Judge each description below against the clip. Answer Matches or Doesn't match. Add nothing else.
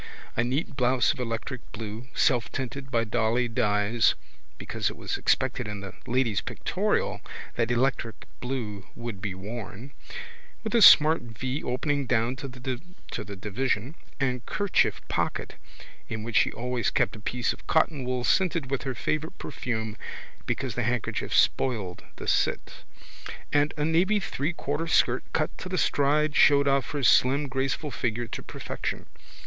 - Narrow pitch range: Doesn't match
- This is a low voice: Matches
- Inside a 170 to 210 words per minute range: Doesn't match